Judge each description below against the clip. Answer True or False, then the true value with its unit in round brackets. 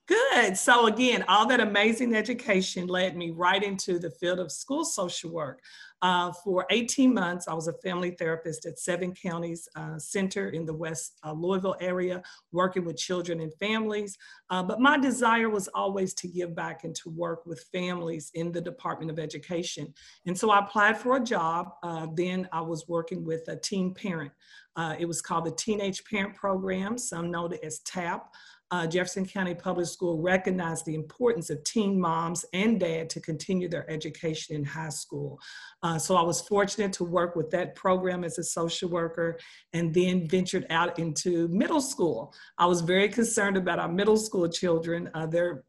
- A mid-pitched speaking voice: True (180 Hz)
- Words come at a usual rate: True (185 wpm)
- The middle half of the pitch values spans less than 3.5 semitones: True (2.8 semitones)